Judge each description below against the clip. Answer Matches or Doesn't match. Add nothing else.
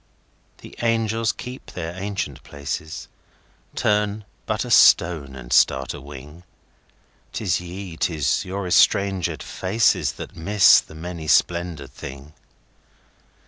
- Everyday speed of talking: Doesn't match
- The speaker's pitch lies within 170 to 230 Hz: Doesn't match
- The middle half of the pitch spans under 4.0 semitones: Doesn't match